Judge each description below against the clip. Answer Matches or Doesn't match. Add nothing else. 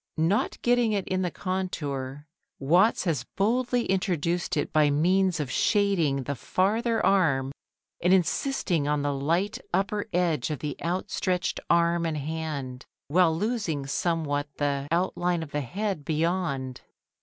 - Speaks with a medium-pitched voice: Matches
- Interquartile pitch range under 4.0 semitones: Doesn't match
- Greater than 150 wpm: Doesn't match